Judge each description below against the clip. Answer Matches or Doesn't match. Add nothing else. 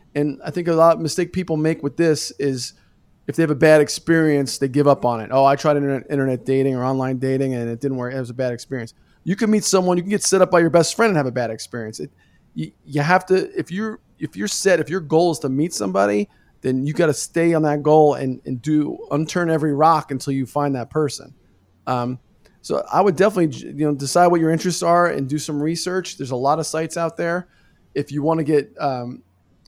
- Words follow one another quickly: Matches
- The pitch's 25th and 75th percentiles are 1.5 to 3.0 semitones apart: Doesn't match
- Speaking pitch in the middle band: Matches